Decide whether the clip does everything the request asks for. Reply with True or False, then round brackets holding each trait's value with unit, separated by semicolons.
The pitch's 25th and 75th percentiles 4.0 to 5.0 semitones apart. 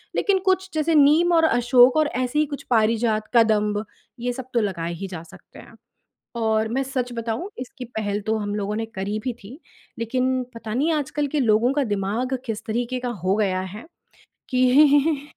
True (4.3 semitones)